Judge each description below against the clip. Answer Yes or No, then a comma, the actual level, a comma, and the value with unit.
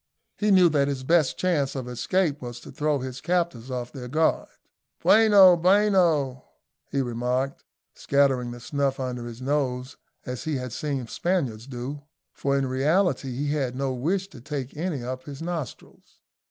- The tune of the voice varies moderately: Yes, average, 4.1 semitones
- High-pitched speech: No, medium, 140 Hz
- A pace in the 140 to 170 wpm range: Yes, average, 165 wpm